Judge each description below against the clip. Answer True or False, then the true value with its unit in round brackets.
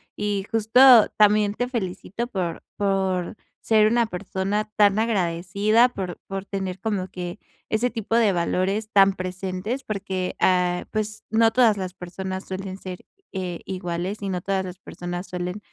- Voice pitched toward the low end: False (195 Hz)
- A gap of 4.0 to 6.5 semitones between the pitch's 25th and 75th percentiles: False (2.7 semitones)